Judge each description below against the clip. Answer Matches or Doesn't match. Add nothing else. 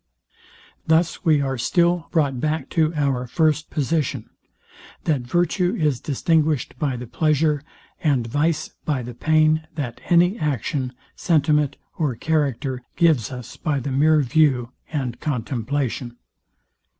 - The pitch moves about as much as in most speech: Matches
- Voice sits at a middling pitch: Matches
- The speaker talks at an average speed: Doesn't match